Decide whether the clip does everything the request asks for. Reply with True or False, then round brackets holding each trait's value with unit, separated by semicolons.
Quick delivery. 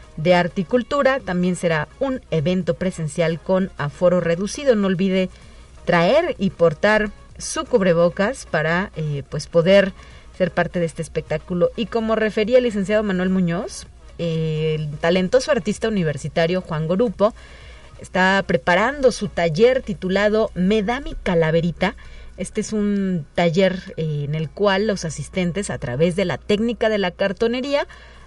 False (145 wpm)